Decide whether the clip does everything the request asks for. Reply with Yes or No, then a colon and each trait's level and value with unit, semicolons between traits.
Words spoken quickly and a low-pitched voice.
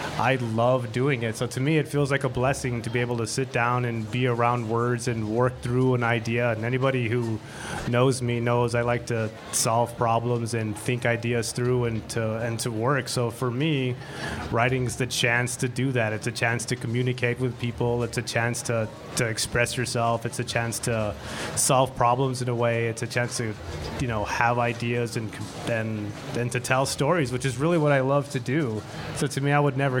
Yes: fast, 215 wpm; low, 120 Hz